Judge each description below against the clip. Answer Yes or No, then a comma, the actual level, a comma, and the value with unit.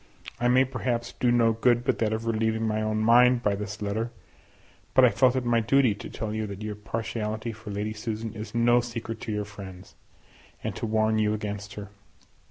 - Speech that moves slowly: No, fast, 205 wpm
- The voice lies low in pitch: Yes, low, 110 Hz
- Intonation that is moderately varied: No, narrow, 1.9 semitones